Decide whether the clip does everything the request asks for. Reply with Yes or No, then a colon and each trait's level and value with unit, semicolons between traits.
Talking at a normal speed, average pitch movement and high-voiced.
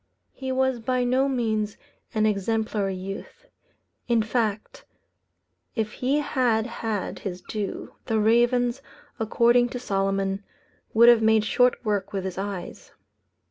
No: slow, 130 wpm; average, 3.2 semitones; high, 220 Hz